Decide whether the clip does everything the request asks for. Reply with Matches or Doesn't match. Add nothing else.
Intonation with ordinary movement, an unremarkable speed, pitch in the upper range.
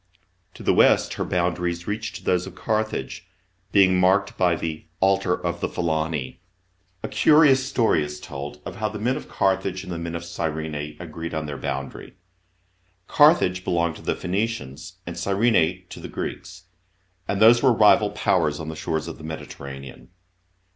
Doesn't match